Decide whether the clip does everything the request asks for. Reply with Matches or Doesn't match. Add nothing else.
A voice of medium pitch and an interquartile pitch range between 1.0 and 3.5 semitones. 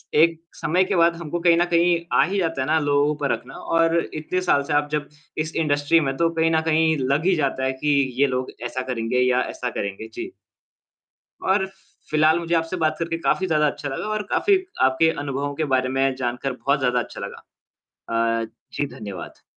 Doesn't match